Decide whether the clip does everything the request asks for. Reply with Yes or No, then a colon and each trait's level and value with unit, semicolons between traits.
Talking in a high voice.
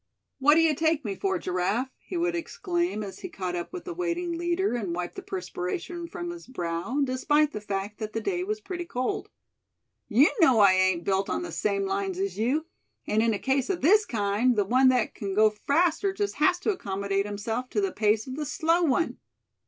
Yes: very high, 270 Hz